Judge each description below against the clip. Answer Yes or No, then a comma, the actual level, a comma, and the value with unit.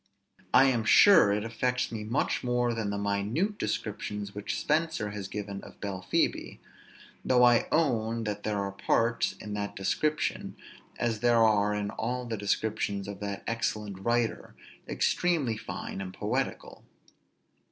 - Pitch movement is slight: No, average, 3.0 semitones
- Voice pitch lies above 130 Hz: No, low, 110 Hz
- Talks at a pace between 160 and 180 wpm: No, average, 145 wpm